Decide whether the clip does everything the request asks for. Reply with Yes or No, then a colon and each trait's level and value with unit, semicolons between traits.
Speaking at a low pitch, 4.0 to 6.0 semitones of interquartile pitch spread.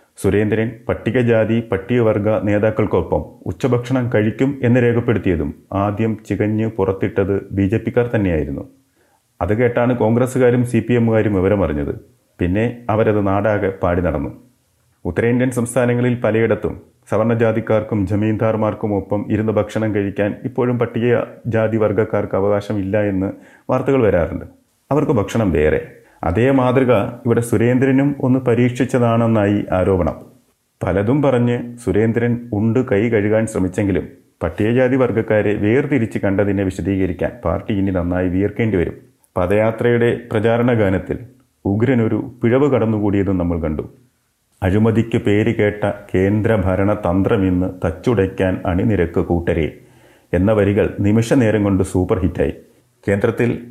No: low, 110 Hz; average, 3.4 semitones